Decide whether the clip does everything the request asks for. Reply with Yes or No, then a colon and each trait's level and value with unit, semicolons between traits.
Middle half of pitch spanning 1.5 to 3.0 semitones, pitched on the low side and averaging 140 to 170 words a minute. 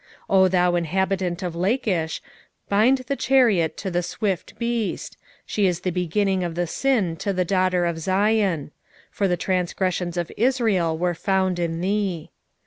No: narrow, 2.6 semitones; medium, 185 Hz; average, 160 wpm